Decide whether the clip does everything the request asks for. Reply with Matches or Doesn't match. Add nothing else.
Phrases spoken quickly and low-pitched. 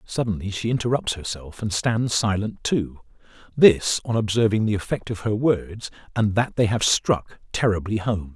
Doesn't match